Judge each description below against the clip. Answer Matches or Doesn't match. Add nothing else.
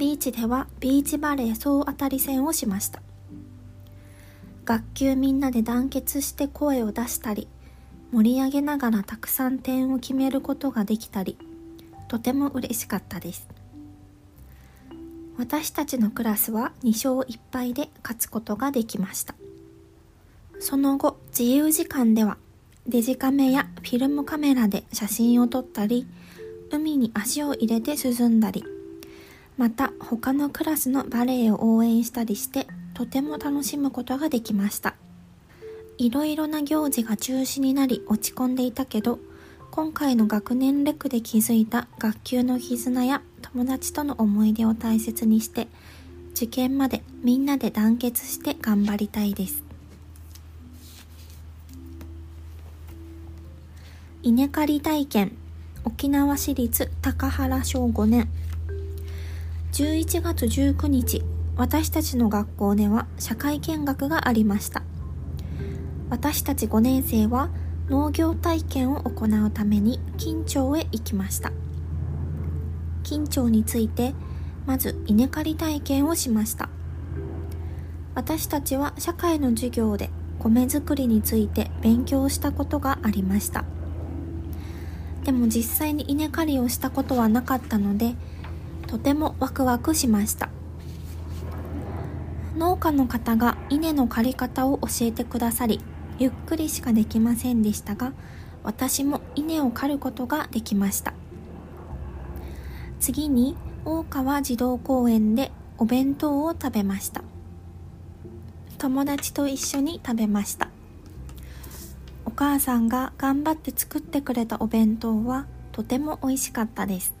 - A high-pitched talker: Matches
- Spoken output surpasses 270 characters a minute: Doesn't match